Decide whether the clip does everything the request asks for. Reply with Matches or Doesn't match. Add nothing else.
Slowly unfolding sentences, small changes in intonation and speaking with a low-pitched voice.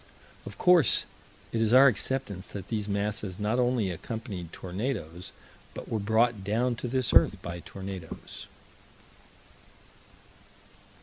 Doesn't match